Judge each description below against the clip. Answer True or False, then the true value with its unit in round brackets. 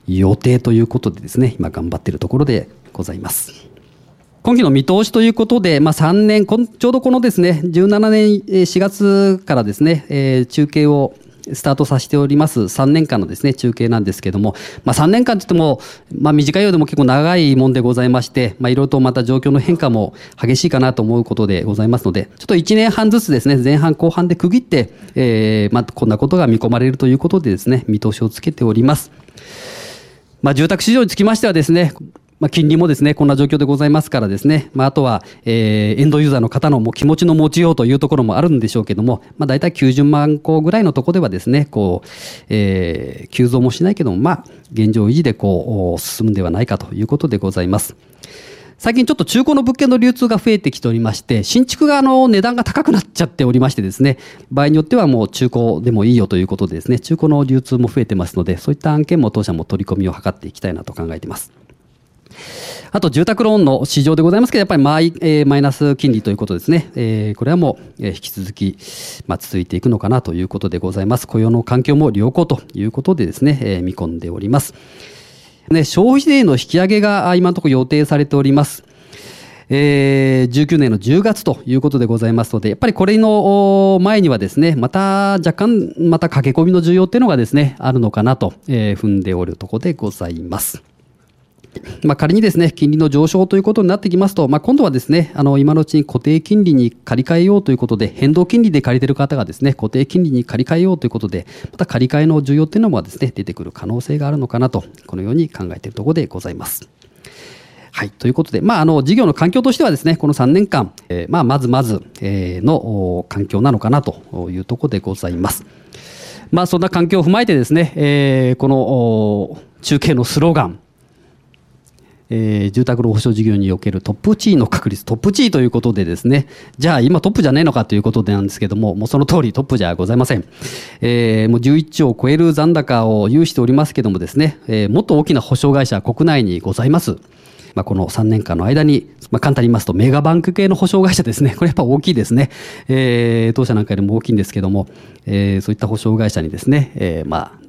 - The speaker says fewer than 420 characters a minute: False (435 characters per minute)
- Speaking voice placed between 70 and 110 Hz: False (135 Hz)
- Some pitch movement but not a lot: False (6.8 semitones)